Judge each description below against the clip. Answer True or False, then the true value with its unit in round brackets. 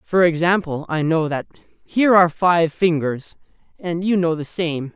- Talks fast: False (170 wpm)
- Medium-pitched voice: True (165 Hz)